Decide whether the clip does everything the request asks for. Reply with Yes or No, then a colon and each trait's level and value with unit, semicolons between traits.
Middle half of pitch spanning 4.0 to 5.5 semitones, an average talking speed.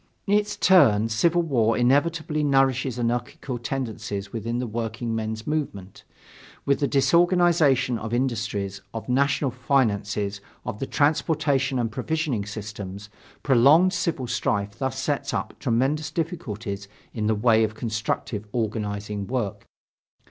No: average, 4.7 semitones; slow, 125 wpm